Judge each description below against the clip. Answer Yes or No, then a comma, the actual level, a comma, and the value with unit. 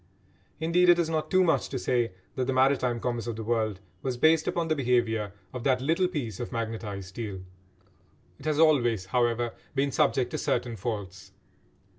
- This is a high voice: No, low, 125 Hz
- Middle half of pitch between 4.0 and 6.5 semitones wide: Yes, average, 4.9 semitones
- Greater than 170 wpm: Yes, average, 180 wpm